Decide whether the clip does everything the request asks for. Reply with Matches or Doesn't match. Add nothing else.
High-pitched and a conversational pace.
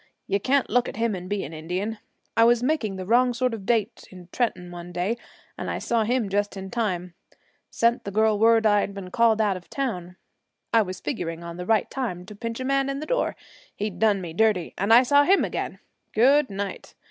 Doesn't match